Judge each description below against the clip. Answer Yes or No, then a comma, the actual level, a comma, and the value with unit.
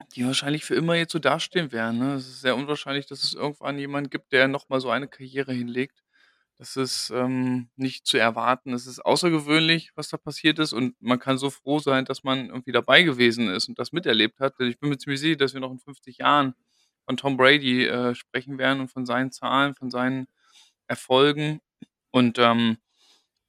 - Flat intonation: Yes, narrow, 2.0 semitones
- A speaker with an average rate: No, fast, 200 wpm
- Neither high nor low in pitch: No, low, 130 Hz